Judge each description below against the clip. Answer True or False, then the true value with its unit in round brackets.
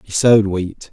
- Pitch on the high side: False (105 Hz)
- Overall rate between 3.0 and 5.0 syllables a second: True (4.9 syllables/s)